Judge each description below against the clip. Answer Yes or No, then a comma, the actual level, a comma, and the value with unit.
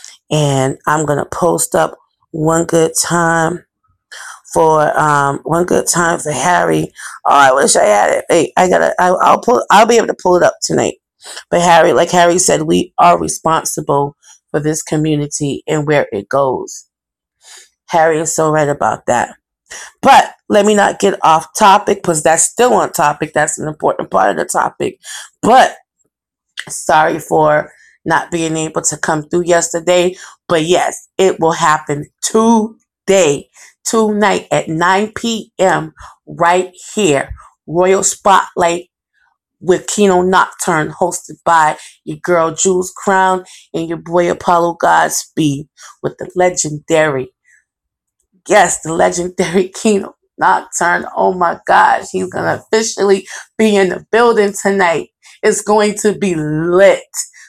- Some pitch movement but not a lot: Yes, average, 3.7 semitones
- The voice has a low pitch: No, medium, 170 Hz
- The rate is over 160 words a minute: No, average, 145 wpm